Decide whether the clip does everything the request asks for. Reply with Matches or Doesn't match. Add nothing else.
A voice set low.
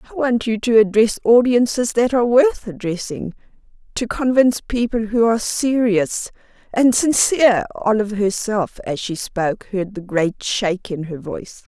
Doesn't match